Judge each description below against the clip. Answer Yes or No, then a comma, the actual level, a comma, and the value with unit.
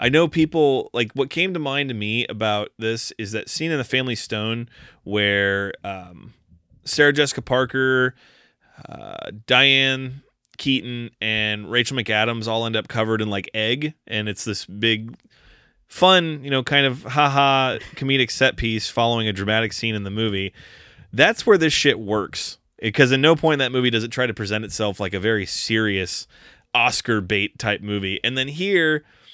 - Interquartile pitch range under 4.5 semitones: Yes, average, 4.0 semitones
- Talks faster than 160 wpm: Yes, average, 175 wpm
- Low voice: Yes, low, 115 Hz